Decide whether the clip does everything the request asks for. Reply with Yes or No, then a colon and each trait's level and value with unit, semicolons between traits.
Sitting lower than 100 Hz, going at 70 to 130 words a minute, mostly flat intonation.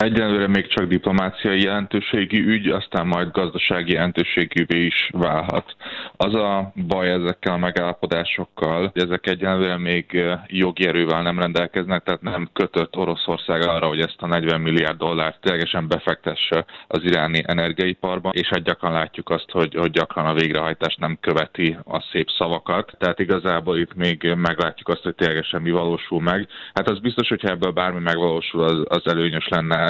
No: very low, 85 Hz; fast, 155 wpm; narrow, 1.9 semitones